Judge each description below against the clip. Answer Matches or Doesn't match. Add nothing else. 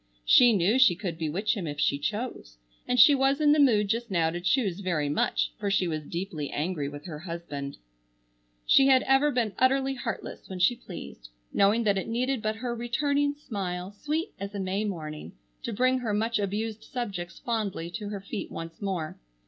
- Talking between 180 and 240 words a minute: Matches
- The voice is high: Matches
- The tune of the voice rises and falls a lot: Matches